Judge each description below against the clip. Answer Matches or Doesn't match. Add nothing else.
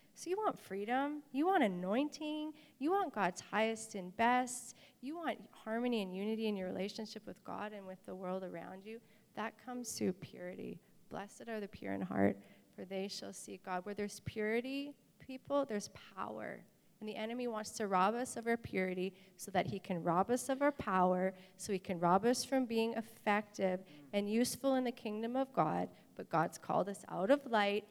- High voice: Matches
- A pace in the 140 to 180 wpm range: Doesn't match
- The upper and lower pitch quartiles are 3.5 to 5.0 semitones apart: Matches